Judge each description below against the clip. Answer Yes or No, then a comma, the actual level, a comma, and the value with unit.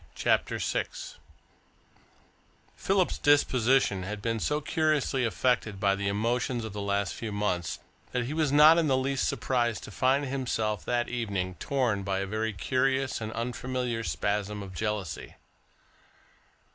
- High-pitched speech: No, low, 115 Hz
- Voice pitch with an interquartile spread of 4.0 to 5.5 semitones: Yes, average, 4.4 semitones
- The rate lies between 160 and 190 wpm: No, average, 145 wpm